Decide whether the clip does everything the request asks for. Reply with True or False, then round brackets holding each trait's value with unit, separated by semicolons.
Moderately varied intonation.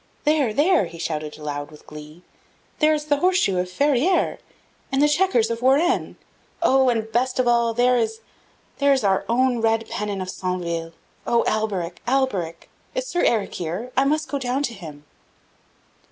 False (7.2 semitones)